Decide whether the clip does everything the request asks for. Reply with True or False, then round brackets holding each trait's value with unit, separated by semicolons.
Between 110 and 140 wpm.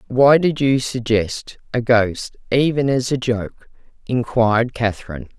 True (135 wpm)